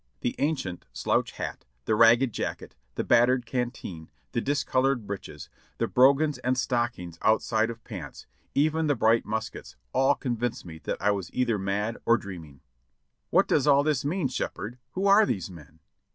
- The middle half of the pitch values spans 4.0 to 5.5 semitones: Yes, average, 4.6 semitones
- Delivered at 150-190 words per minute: Yes, average, 165 wpm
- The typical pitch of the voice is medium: No, low, 120 Hz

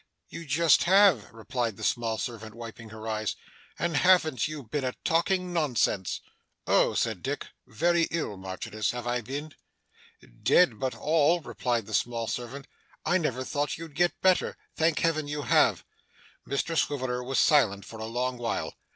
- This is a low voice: Yes, low, 130 Hz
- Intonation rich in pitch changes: Yes, wide, 5.8 semitones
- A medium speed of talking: Yes, average, 160 wpm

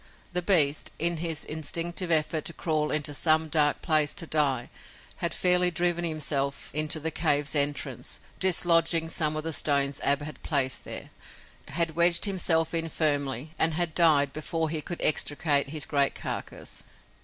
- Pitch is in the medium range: Yes, medium, 155 Hz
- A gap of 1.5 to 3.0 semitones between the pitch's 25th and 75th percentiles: Yes, narrow, 2.4 semitones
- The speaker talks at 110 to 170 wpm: Yes, average, 160 wpm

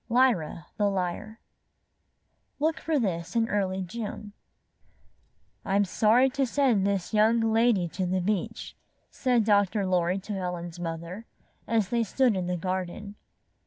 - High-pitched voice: Yes, high, 205 Hz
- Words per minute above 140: No, slow, 135 wpm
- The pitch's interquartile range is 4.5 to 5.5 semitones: No, average, 3.9 semitones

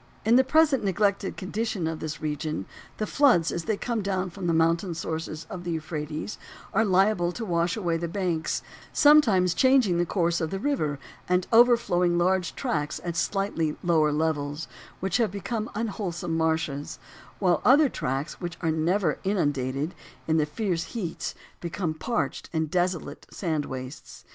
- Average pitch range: Yes, average, 4.1 semitones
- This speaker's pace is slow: No, average, 165 wpm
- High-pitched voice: No, medium, 175 Hz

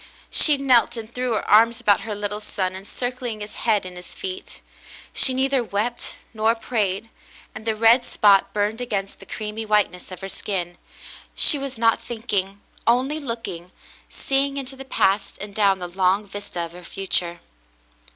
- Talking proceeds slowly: No, average, 170 wpm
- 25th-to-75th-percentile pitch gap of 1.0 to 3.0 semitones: No, average, 3.9 semitones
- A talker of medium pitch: No, high, 215 Hz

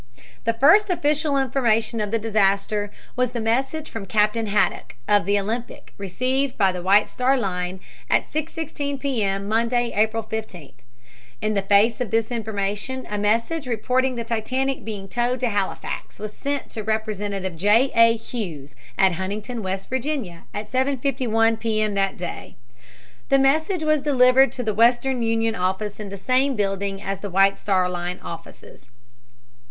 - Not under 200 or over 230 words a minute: No, average, 160 wpm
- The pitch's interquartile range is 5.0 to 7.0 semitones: No, average, 4.3 semitones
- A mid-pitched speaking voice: No, high, 225 Hz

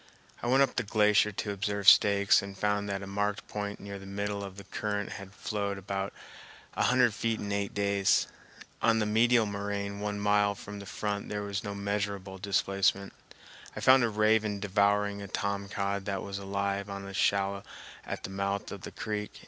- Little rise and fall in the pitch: Yes, narrow, 0.8 semitones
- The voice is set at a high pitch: No, low, 100 Hz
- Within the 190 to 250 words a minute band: Yes, average, 195 wpm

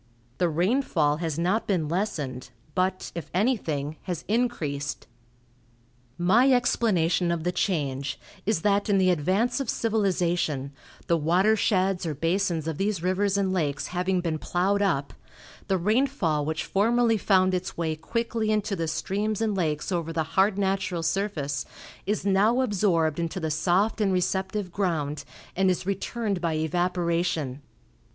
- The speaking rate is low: No, average, 145 wpm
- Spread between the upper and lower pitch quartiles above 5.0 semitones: No, average, 4.0 semitones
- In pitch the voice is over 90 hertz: Yes, medium, 185 Hz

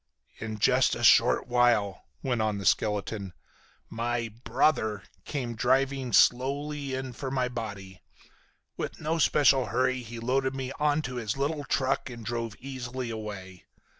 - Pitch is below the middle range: Yes, low, 125 Hz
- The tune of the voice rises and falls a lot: No, average, 3.4 semitones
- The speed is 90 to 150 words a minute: Yes, average, 140 wpm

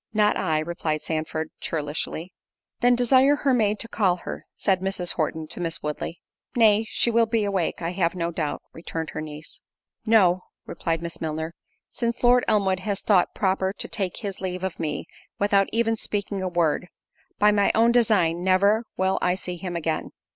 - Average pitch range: Yes, average, 4.2 semitones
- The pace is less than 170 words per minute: No, average, 180 wpm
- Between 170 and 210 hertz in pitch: Yes, medium, 185 Hz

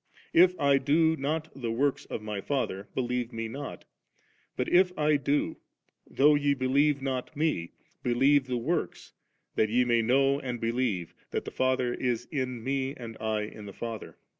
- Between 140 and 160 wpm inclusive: No, average, 170 wpm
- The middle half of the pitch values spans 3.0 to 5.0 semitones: Yes, average, 3.5 semitones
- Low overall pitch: Yes, low, 130 Hz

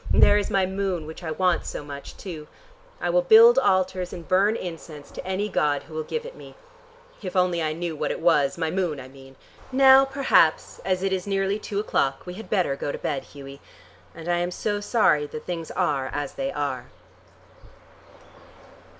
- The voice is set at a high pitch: No, medium, 175 Hz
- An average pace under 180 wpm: No, average, 195 wpm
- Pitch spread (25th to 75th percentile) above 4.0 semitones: Yes, average, 4.6 semitones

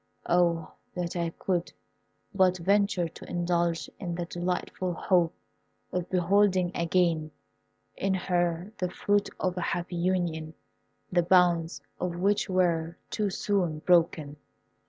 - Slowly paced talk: Yes, slow, 125 wpm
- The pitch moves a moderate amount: No, narrow, 1.6 semitones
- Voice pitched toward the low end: No, medium, 175 Hz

